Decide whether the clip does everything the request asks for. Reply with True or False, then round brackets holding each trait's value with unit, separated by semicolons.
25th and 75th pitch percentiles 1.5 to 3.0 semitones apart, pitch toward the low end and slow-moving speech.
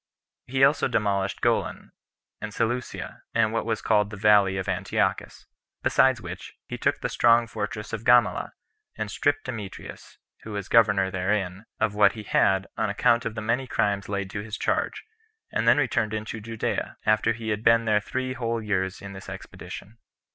False (2.4 semitones; 110 Hz; 175 wpm)